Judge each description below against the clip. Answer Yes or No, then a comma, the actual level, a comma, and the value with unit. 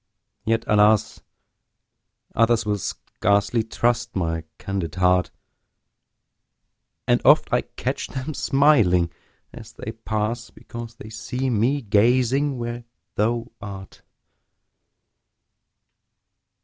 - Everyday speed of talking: No, slow, 95 wpm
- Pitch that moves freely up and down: No, average, 2.9 semitones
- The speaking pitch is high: No, low, 110 Hz